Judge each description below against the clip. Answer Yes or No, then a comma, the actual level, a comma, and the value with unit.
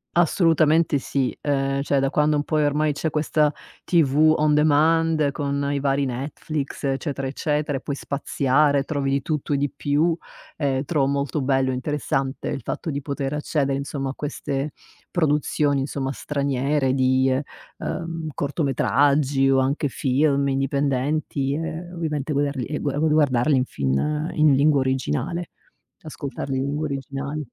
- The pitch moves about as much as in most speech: No, narrow, 1.9 semitones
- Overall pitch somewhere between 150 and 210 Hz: No, medium, 140 Hz